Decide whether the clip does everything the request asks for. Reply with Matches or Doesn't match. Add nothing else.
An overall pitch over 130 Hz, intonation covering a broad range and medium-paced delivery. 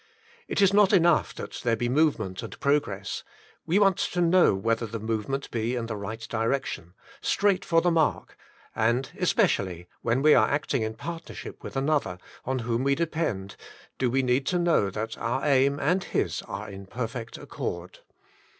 Doesn't match